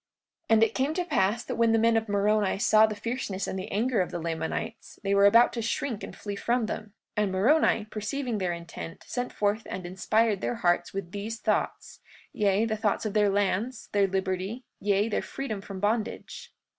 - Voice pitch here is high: Yes, high, 210 Hz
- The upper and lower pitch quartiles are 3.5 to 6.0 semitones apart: No, average, 2.7 semitones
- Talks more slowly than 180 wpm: No, average, 200 wpm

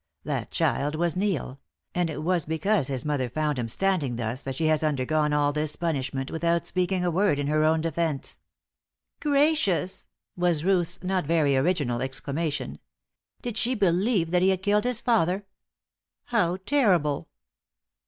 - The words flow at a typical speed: Yes, average, 155 wpm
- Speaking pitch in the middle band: Yes, medium, 165 Hz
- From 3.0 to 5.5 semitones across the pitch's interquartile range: Yes, average, 4.3 semitones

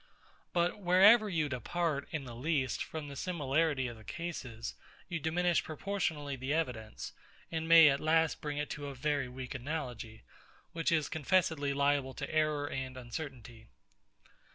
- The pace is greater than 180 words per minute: No, average, 155 wpm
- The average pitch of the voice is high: No, medium, 145 Hz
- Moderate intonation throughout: Yes, average, 3.7 semitones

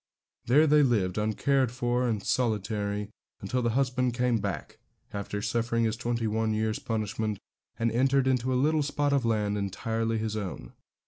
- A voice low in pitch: Yes, low, 115 Hz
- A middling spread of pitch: Yes, average, 3.0 semitones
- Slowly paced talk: No, average, 165 wpm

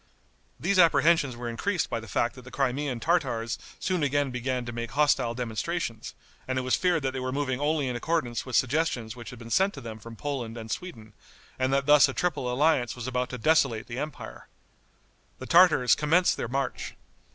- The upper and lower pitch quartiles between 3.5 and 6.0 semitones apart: Yes, average, 4.0 semitones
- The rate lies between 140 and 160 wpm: No, average, 200 wpm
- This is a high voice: No, low, 130 Hz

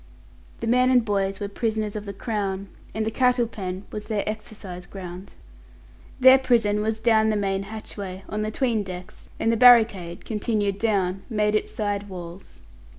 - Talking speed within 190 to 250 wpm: No, average, 170 wpm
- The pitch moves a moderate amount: No, narrow, 2.3 semitones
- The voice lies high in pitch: Yes, high, 210 Hz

